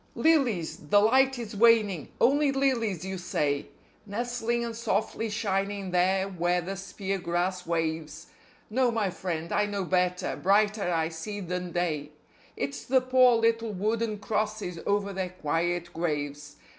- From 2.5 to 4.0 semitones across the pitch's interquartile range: No, average, 4.5 semitones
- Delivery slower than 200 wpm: Yes, average, 145 wpm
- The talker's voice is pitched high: Yes, high, 195 Hz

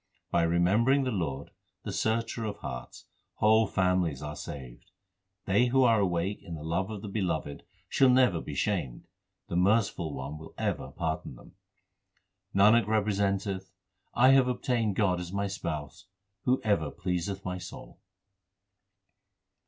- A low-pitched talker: Yes, very low, 95 Hz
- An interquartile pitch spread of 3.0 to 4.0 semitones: No, average, 4.7 semitones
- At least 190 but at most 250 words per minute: No, average, 145 wpm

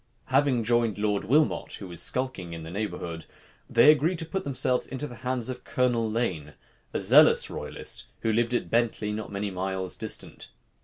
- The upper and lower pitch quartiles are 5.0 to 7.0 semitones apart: No, average, 4.5 semitones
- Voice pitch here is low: Yes, low, 115 Hz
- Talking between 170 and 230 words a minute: Yes, average, 175 wpm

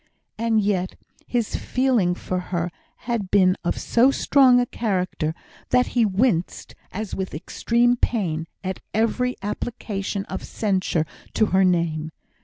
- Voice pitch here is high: Yes, high, 200 Hz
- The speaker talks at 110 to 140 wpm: Yes, slow, 135 wpm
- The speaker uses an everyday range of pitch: Yes, average, 4.5 semitones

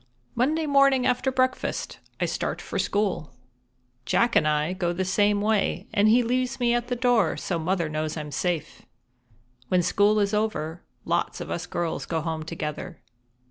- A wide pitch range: Yes, wide, 6.7 semitones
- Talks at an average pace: Yes, average, 175 wpm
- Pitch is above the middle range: Yes, high, 200 Hz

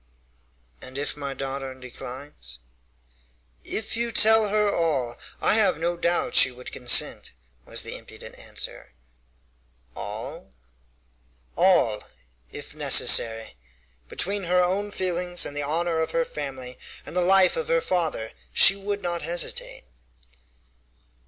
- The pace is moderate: No, slow, 125 wpm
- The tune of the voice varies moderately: No, wide, 6.3 semitones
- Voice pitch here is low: No, medium, 170 Hz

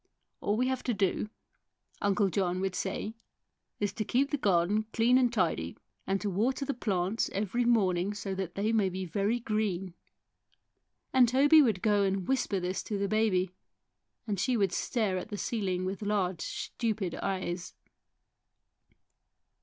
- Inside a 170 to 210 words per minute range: No, average, 160 wpm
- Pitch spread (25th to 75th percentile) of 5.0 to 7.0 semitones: No, average, 3.2 semitones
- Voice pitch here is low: No, high, 200 Hz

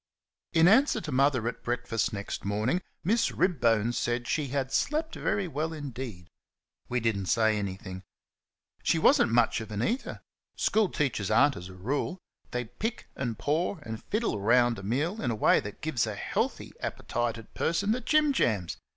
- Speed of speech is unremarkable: Yes, average, 180 wpm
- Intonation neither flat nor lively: No, wide, 6.8 semitones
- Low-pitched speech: Yes, low, 125 Hz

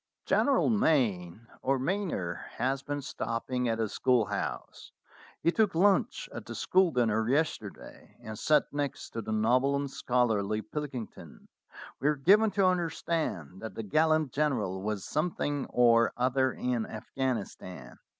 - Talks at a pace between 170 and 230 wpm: No, average, 140 wpm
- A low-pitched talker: Yes, low, 130 Hz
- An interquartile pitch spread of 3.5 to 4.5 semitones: No, wide, 5.6 semitones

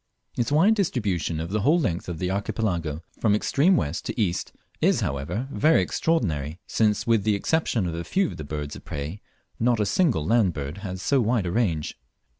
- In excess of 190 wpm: Yes, average, 200 wpm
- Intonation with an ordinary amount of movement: No, wide, 6.6 semitones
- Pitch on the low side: Yes, low, 100 Hz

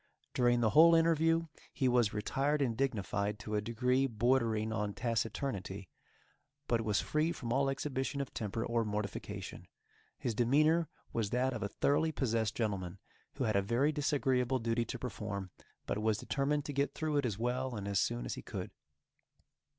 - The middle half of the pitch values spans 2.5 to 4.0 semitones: No, average, 4.4 semitones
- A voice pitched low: Yes, low, 120 Hz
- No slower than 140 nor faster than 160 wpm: No, average, 175 wpm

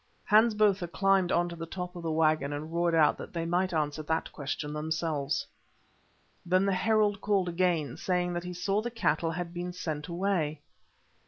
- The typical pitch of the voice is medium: Yes, medium, 175 Hz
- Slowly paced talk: No, average, 185 wpm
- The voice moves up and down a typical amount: Yes, average, 3.0 semitones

